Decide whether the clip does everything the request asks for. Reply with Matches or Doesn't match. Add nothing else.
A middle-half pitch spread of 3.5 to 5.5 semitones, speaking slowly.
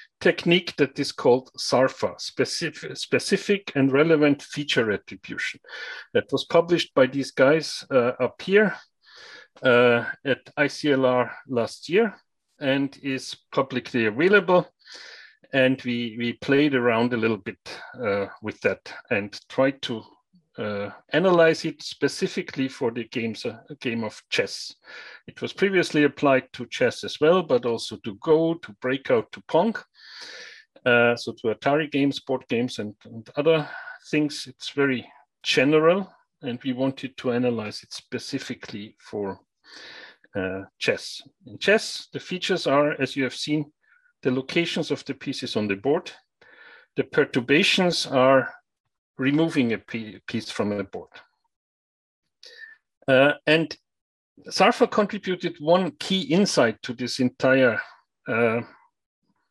Matches